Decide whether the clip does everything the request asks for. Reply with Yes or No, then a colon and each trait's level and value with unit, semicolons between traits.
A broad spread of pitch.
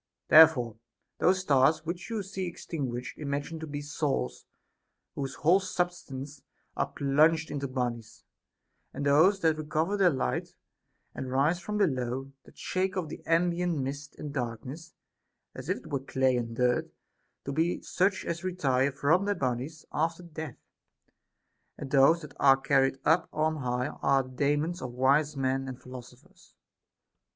No: average, 3.8 semitones